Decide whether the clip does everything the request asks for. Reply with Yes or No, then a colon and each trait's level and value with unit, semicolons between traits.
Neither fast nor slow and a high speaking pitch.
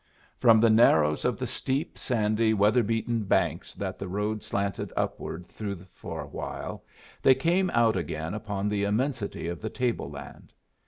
No: average, 165 wpm; low, 105 Hz